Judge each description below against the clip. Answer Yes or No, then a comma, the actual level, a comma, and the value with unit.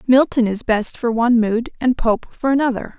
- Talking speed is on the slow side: No, average, 200 wpm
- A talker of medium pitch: No, high, 235 Hz